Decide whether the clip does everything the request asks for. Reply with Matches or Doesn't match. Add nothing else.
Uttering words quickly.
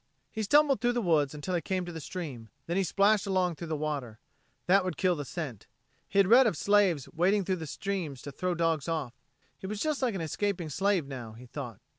Matches